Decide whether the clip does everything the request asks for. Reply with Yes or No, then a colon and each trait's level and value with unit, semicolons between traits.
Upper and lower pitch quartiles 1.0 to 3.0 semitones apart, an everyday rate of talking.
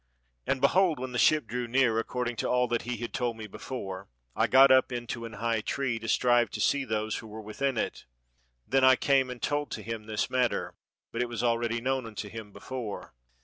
No: narrow, 2.5 semitones; fast, 220 wpm